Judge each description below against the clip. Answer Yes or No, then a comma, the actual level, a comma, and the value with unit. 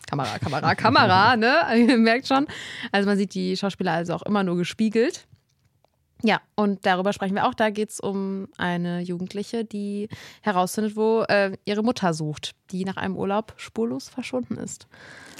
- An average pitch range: Yes, average, 3.1 semitones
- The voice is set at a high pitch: Yes, high, 205 Hz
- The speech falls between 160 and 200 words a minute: Yes, average, 170 wpm